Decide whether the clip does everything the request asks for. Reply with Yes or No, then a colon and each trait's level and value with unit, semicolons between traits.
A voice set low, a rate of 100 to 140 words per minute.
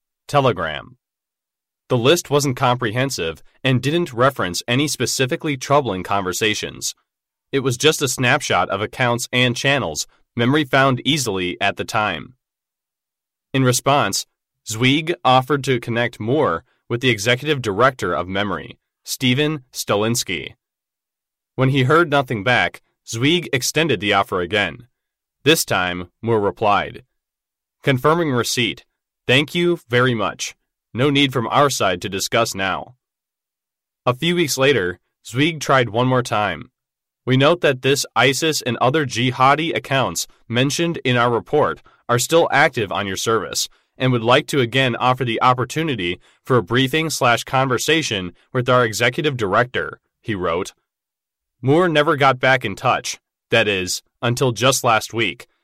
Yes: low, 130 Hz; slow, 135 wpm